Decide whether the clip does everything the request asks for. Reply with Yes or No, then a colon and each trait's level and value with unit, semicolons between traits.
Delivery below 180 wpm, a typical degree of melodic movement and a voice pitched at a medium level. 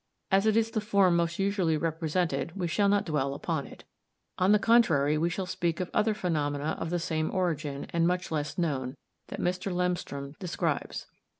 No: average, 185 wpm; average, 3.5 semitones; medium, 170 Hz